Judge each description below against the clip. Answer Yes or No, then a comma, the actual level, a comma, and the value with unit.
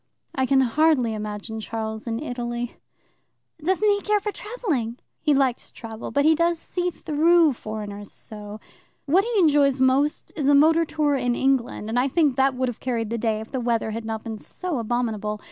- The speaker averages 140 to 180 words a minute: No, average, 190 wpm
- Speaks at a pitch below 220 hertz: No, very high, 260 Hz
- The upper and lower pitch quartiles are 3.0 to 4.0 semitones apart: No, wide, 5.4 semitones